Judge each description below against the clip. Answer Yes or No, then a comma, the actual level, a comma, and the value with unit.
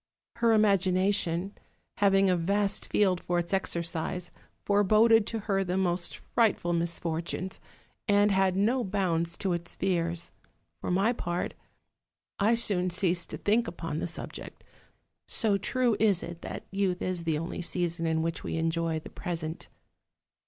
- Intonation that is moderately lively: Yes, average, 3.0 semitones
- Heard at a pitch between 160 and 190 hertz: Yes, medium, 185 Hz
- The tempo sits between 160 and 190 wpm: No, average, 145 wpm